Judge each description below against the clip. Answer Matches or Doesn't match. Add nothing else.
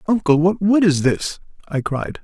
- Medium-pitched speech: Matches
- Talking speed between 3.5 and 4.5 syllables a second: Matches